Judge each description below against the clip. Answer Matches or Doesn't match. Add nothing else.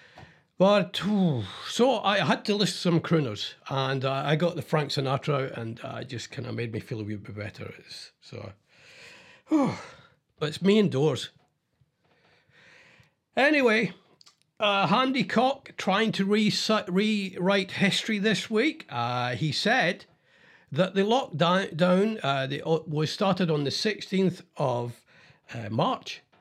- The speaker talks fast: Doesn't match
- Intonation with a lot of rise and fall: Matches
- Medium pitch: Matches